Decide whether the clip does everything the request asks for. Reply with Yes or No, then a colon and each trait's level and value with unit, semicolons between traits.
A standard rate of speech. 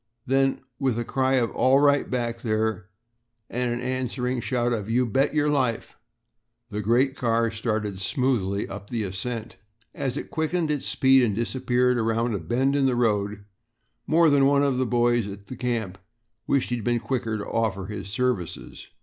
Yes: average, 180 wpm